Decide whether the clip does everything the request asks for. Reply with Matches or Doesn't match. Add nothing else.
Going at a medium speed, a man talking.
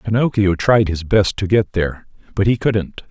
Matches